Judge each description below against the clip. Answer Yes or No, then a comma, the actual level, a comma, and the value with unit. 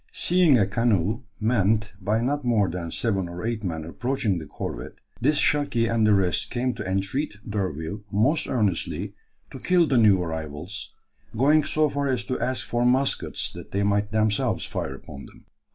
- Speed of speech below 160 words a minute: No, average, 175 wpm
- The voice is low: Yes, low, 110 Hz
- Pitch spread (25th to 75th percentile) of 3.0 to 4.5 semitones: No, average, 5.1 semitones